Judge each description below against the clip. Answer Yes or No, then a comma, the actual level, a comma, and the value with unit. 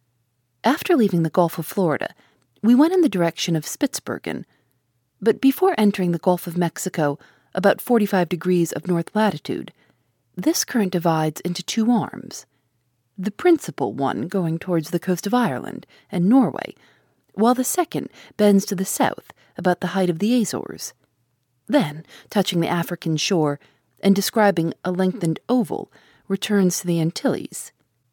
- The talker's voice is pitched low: No, medium, 180 Hz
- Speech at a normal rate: Yes, average, 150 wpm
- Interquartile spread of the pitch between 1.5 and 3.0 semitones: No, average, 4.8 semitones